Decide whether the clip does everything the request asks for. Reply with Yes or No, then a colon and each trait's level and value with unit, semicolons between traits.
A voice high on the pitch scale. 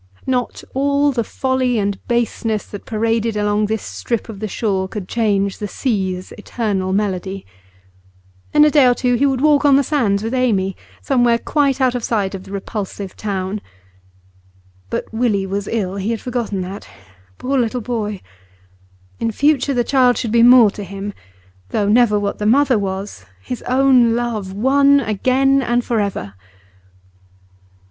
Yes: high, 225 Hz